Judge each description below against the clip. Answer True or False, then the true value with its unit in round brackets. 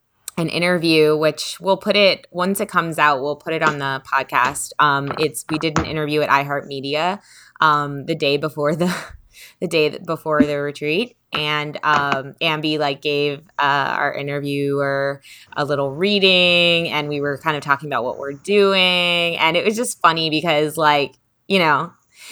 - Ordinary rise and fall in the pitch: True (3.1 semitones)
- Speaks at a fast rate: False (170 wpm)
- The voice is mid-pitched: True (155 Hz)